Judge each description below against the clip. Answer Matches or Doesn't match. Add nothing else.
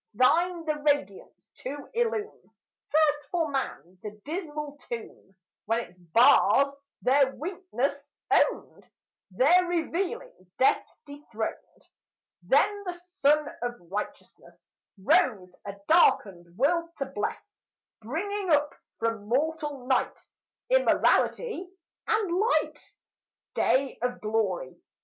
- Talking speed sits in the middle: Doesn't match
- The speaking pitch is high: Matches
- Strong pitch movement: Matches